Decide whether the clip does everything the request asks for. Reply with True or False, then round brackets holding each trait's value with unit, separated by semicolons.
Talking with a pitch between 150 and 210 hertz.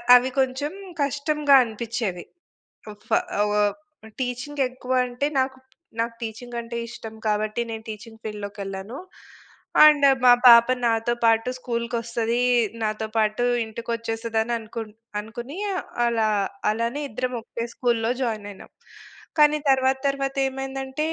False (235 Hz)